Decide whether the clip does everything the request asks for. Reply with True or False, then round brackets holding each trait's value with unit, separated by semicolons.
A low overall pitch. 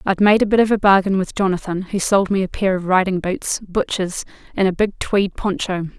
False (190 Hz)